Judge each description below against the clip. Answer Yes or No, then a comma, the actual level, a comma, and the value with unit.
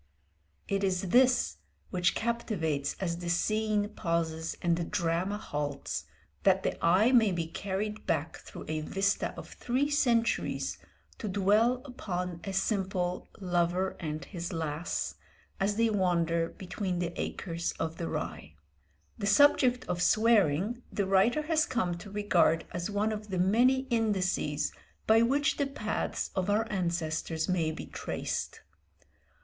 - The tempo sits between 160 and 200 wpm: No, average, 145 wpm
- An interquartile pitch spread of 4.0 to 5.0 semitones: Yes, average, 4.4 semitones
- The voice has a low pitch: No, high, 190 Hz